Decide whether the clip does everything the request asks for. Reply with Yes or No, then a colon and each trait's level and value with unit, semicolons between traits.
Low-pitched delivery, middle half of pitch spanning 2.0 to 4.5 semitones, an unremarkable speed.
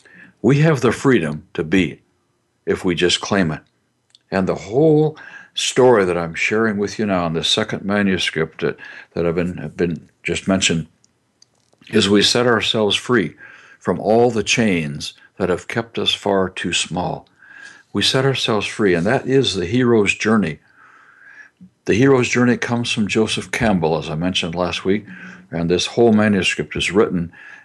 No: low, 100 Hz; average, 5.2 semitones; average, 165 wpm